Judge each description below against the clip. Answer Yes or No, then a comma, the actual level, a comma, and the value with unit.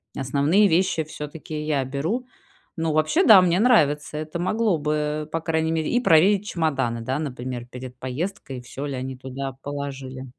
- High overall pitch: No, medium, 150 Hz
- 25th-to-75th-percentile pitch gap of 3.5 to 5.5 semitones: Yes, average, 4.1 semitones